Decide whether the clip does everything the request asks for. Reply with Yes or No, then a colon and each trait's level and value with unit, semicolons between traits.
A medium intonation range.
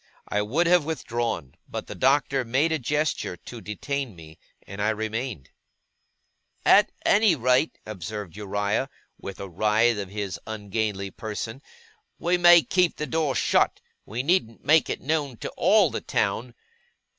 No: wide, 6.2 semitones